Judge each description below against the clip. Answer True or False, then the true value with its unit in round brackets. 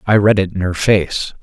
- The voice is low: True (95 Hz)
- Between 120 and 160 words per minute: False (255 wpm)